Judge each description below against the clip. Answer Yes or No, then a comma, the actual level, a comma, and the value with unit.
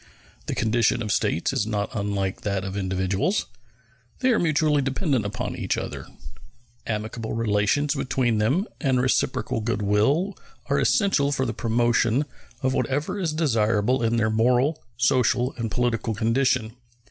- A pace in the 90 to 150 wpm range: Yes, average, 145 wpm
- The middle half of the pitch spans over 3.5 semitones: Yes, average, 4.3 semitones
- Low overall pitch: Yes, low, 120 Hz